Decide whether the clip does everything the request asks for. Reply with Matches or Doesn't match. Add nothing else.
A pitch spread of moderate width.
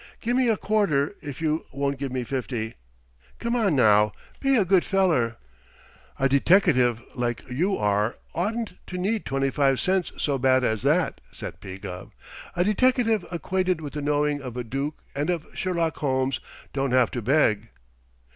Doesn't match